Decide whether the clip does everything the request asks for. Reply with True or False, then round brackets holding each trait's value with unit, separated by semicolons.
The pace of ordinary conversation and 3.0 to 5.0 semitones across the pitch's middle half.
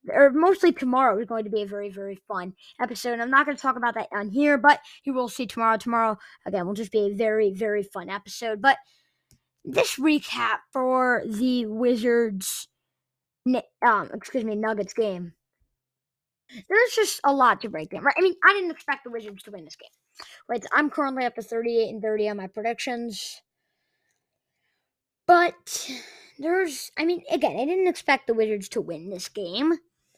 False (185 wpm; 5.6 semitones)